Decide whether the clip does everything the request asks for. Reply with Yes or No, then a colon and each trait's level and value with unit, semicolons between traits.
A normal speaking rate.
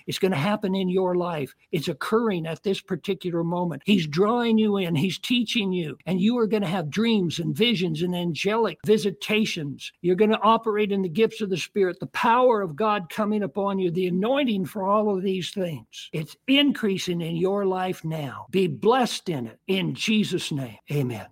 Yes: average, 195 wpm